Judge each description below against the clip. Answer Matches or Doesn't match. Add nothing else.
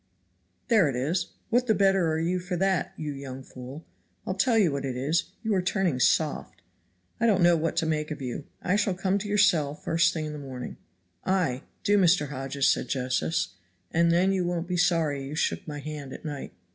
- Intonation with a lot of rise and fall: Doesn't match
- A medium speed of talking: Doesn't match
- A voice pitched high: Doesn't match